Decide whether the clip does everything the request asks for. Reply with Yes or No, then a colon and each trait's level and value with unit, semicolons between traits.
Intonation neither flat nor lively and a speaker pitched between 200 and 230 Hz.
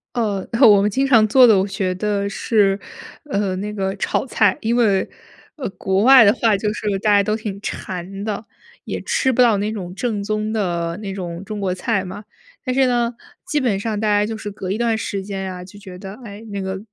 No: narrow, 2.3 semitones; high, 205 Hz